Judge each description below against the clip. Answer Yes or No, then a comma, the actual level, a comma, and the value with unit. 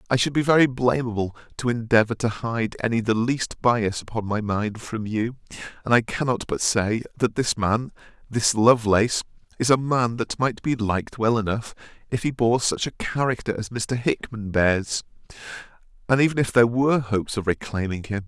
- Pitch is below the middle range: Yes, low, 115 Hz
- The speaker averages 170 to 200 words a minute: Yes, average, 175 wpm